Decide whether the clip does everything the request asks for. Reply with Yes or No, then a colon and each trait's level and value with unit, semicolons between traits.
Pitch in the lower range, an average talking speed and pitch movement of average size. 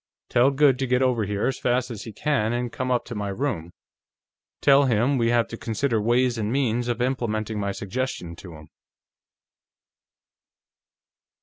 Yes: low, 120 Hz; average, 170 wpm; average, 3.1 semitones